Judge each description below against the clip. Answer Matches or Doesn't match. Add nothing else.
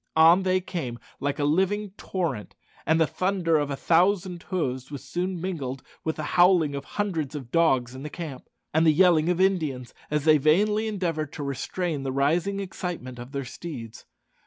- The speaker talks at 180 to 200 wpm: Matches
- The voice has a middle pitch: Matches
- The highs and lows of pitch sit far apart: Doesn't match